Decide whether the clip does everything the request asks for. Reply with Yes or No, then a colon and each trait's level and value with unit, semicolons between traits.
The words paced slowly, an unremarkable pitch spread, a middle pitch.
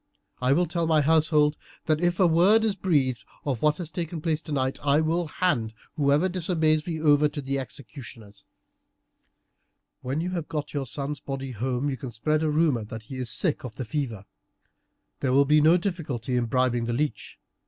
No: average, 190 wpm; average, 3.9 semitones; medium, 150 Hz